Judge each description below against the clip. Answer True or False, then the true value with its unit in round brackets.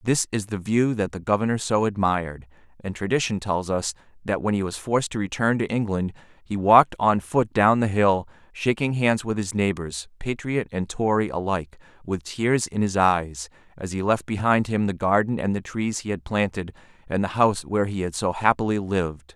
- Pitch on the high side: False (100 Hz)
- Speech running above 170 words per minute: True (200 wpm)